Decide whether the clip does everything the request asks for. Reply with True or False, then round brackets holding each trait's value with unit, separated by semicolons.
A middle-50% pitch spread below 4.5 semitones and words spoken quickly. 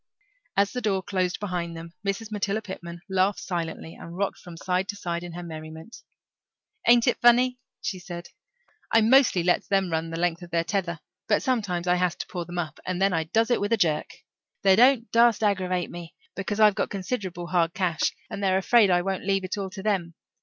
True (3.0 semitones; 210 wpm)